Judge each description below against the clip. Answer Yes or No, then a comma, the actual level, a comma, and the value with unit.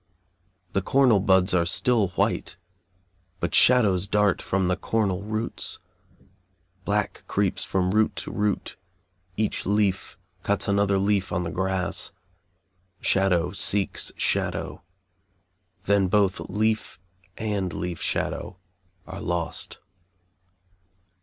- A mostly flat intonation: Yes, narrow, 2.1 semitones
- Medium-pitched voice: No, low, 100 Hz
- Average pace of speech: No, slow, 105 wpm